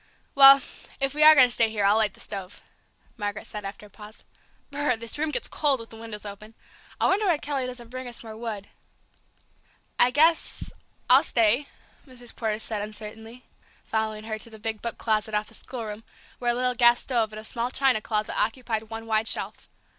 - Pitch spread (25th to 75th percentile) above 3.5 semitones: No, average, 2.8 semitones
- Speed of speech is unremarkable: No, fast, 210 wpm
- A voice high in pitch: Yes, high, 225 Hz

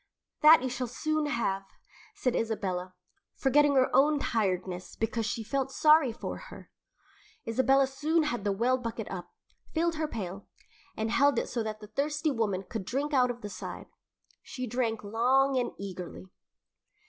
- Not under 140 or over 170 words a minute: Yes, average, 165 wpm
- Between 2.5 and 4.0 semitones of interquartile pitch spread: No, average, 4.7 semitones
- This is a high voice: Yes, high, 245 Hz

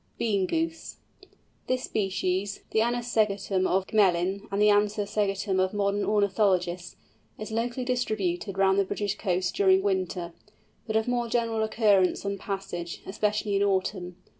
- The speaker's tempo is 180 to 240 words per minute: No, average, 145 wpm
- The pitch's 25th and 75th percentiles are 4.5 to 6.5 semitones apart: No, narrow, 2.5 semitones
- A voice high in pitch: Yes, high, 200 Hz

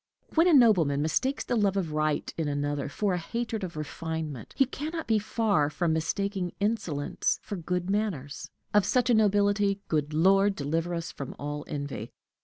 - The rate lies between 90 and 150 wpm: No, average, 180 wpm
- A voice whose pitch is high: No, medium, 180 Hz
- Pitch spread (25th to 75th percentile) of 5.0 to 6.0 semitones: Yes, wide, 5.5 semitones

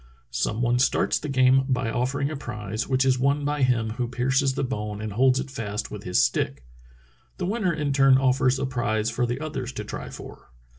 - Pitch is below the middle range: Yes, low, 130 Hz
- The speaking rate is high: Yes, fast, 210 wpm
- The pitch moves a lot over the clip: No, average, 3.2 semitones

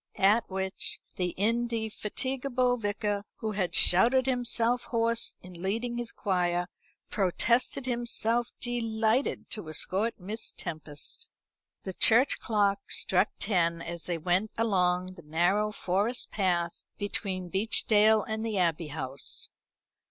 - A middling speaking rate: No, slow, 120 wpm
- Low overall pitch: No, high, 205 Hz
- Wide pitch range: No, average, 4.3 semitones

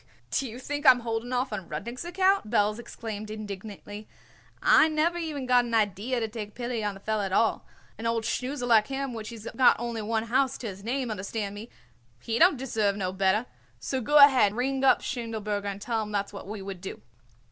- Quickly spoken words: Yes, fast, 215 wpm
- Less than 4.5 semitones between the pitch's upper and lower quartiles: Yes, average, 3.6 semitones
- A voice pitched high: Yes, high, 225 Hz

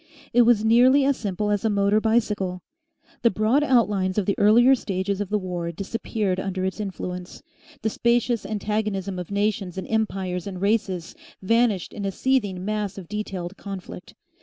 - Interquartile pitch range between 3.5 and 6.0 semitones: No, average, 2.8 semitones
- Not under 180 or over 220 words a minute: No, average, 165 wpm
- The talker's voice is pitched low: No, high, 205 Hz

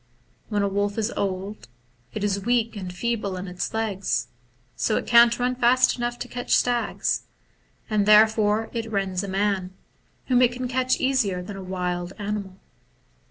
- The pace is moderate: Yes, average, 165 wpm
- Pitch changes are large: No, average, 3.5 semitones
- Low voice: No, high, 210 Hz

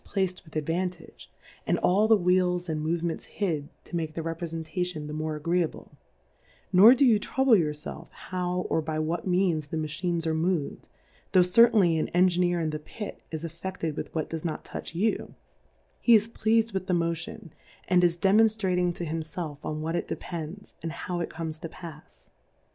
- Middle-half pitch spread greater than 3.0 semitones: No, narrow, 2.6 semitones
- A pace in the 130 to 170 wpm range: No, average, 185 wpm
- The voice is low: No, medium, 170 Hz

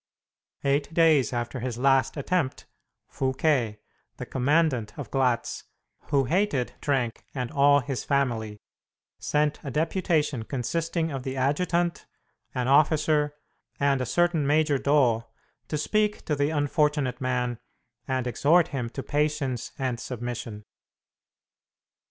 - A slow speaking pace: Yes, slow, 120 wpm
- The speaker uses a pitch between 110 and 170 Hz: Yes, medium, 140 Hz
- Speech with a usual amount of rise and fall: Yes, average, 3.3 semitones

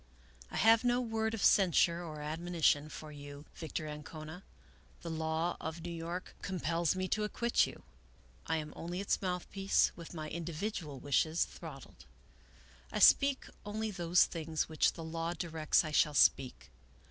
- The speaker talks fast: No, average, 155 wpm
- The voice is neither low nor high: Yes, medium, 165 Hz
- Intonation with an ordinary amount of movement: Yes, average, 3.2 semitones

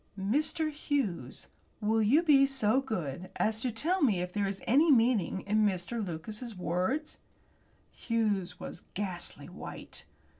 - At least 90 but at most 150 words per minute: Yes, average, 140 wpm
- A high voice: Yes, high, 220 Hz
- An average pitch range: No, wide, 6.2 semitones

